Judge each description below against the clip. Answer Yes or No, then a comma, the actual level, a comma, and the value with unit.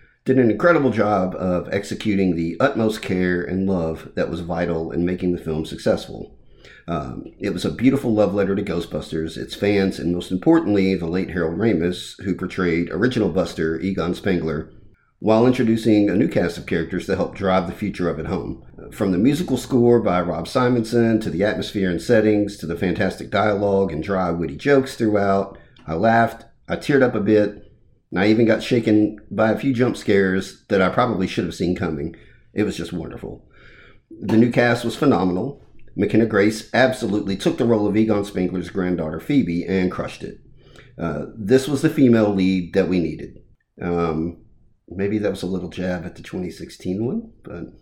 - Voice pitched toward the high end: No, low, 100 Hz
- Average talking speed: Yes, average, 185 wpm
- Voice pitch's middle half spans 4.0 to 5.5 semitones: Yes, average, 4.3 semitones